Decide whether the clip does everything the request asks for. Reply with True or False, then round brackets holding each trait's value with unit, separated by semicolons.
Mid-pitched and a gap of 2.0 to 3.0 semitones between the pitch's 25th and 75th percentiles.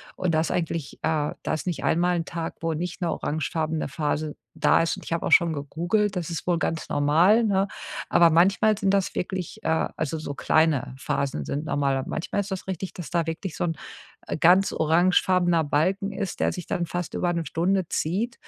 True (170 Hz; 2.7 semitones)